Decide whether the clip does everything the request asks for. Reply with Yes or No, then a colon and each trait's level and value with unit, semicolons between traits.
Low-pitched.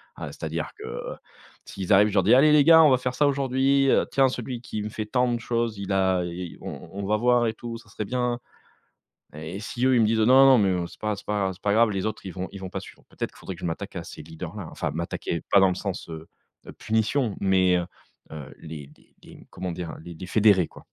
Yes: low, 105 Hz